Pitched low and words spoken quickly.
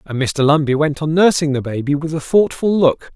No: medium, 150 Hz; fast, 230 wpm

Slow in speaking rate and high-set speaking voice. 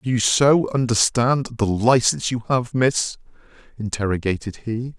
No: slow, 130 wpm; low, 120 Hz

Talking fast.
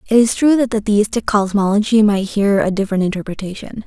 No: average, 185 wpm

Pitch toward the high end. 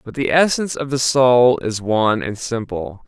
No: low, 120 Hz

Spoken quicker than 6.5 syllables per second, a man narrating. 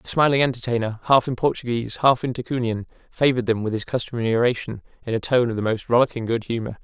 Yes: 7.0 syllables/s; male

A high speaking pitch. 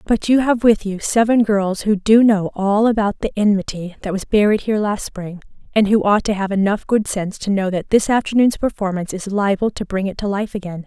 Yes: high, 205 Hz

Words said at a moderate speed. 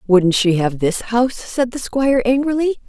Yes: average, 190 wpm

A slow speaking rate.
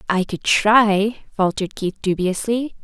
Yes: slow, 125 wpm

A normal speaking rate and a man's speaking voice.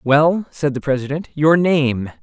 Yes: average, 160 wpm; male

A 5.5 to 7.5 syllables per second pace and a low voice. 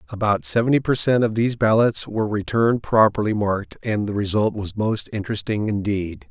Yes: 5.7 syllables/s; low, 110 Hz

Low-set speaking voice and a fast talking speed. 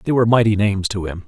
Yes: low, 105 Hz; fast, 280 wpm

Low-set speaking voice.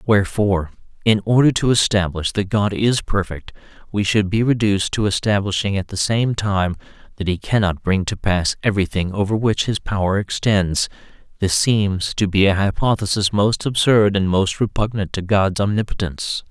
Yes: low, 100 Hz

